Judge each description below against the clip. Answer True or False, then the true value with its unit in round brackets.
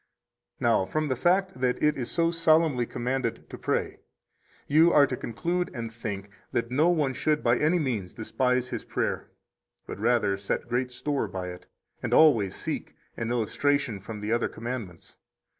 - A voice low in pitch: True (125 Hz)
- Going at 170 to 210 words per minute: True (175 wpm)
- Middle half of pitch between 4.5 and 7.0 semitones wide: True (5.0 semitones)